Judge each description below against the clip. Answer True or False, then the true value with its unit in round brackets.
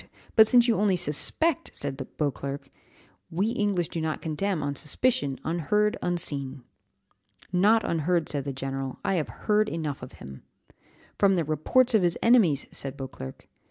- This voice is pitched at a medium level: True (165 Hz)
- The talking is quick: False (155 wpm)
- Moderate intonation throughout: False (6.7 semitones)